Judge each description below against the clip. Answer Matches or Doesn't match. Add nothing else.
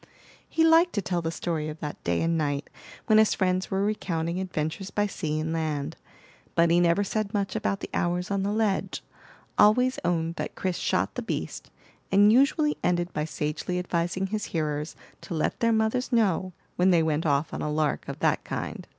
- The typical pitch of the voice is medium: Matches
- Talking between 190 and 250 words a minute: Matches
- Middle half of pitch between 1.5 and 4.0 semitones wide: Doesn't match